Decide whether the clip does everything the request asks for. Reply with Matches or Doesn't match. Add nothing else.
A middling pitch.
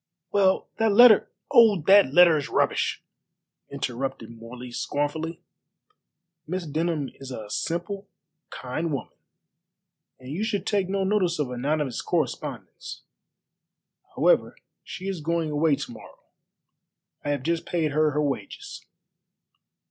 Matches